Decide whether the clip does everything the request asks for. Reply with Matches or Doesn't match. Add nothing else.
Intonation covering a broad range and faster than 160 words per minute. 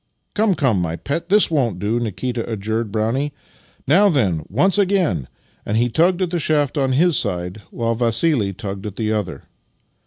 Matches